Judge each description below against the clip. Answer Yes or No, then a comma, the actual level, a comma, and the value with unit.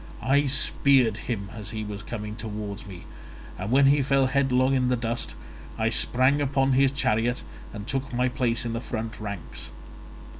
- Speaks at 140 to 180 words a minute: Yes, average, 175 wpm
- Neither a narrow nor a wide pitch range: Yes, average, 3.8 semitones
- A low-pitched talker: Yes, low, 120 Hz